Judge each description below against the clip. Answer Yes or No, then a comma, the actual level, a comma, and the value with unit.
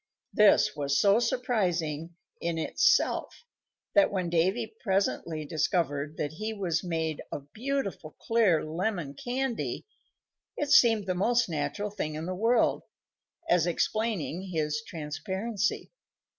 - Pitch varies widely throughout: Yes, wide, 5.8 semitones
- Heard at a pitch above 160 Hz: Yes, medium, 185 Hz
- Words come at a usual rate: No, slow, 120 wpm